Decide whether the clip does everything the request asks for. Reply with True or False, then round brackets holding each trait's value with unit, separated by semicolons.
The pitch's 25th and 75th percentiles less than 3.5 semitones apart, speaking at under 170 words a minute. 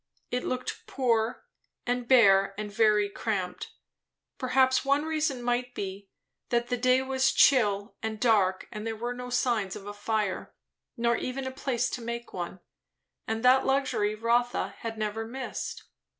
True (3.1 semitones; 155 wpm)